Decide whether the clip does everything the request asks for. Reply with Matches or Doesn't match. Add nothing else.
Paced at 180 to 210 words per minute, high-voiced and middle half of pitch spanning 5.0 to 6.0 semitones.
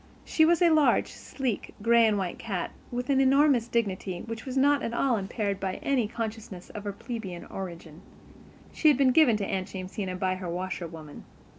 Matches